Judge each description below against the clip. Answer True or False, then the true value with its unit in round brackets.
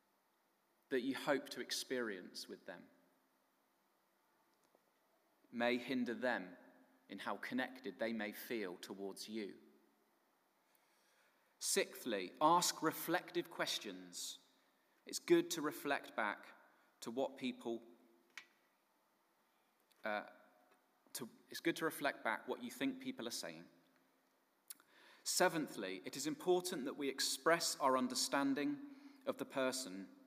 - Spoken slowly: True (110 wpm)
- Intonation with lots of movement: True (7.4 semitones)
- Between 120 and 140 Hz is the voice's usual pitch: True (135 Hz)